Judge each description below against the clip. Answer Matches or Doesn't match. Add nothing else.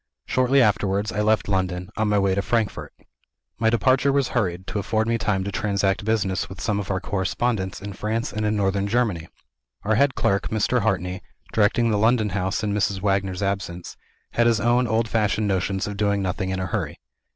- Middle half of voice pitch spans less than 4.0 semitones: Matches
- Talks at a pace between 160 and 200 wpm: Matches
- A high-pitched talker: Doesn't match